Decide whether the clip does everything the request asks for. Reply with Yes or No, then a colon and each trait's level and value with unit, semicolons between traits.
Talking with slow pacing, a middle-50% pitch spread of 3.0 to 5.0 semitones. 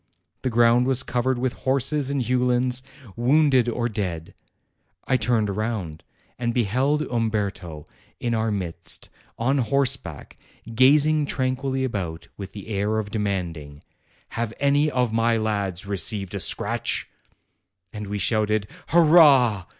Yes: slow, 125 wpm; average, 4.2 semitones